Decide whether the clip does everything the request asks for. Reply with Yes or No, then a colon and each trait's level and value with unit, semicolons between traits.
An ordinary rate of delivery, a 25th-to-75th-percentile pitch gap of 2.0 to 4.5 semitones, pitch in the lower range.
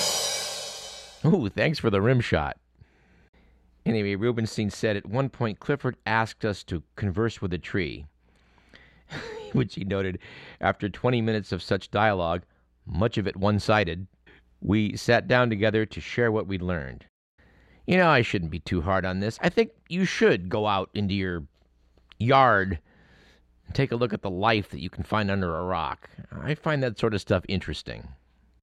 No: average, 170 wpm; average, 5.2 semitones; low, 100 Hz